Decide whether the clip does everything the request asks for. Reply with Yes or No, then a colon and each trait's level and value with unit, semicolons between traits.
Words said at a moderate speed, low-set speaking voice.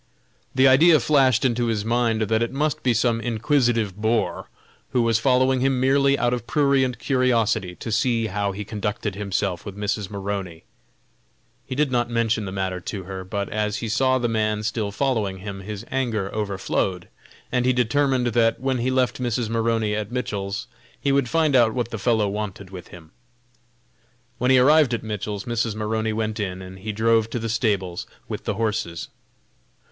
Yes: average, 180 wpm; low, 115 Hz